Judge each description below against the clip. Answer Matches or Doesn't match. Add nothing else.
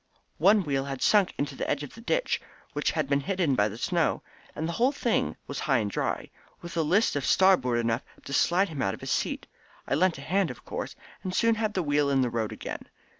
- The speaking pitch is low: Doesn't match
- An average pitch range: Doesn't match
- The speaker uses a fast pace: Matches